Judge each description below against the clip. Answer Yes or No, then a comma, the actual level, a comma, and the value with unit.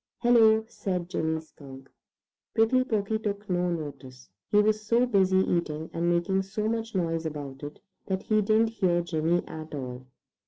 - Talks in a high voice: No, medium, 180 Hz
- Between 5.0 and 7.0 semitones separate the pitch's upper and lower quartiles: Yes, average, 5.3 semitones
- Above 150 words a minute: Yes, average, 160 wpm